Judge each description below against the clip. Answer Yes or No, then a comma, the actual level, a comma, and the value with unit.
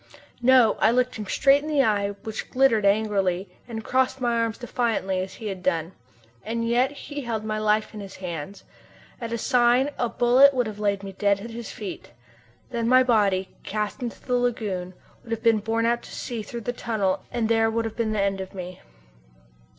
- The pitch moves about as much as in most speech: Yes, average, 3.2 semitones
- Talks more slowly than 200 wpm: No, fast, 205 wpm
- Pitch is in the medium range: No, high, 225 Hz